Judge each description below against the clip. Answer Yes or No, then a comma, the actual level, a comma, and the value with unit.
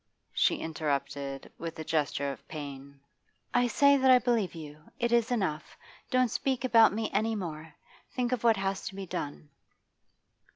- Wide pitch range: Yes, wide, 7.9 semitones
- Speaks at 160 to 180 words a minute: Yes, average, 165 wpm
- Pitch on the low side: No, high, 195 Hz